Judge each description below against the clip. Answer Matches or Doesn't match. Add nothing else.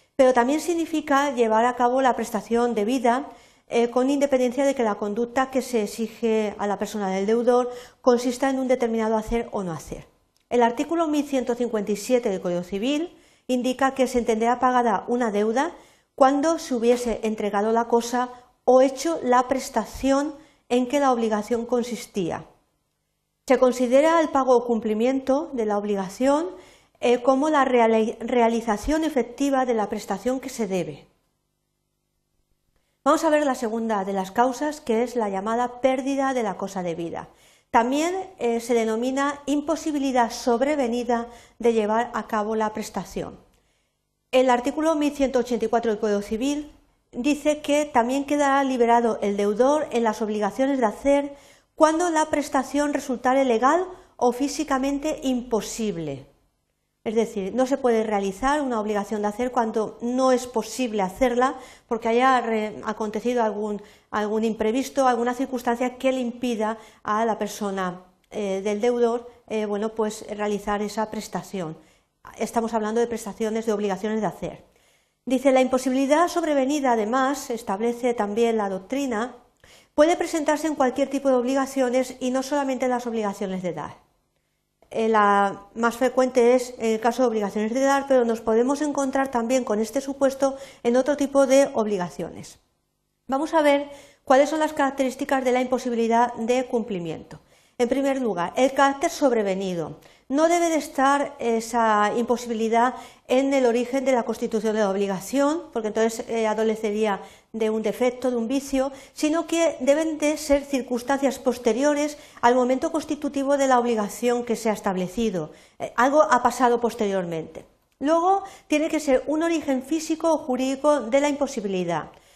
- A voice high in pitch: Matches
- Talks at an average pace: Matches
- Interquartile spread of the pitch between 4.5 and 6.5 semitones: Doesn't match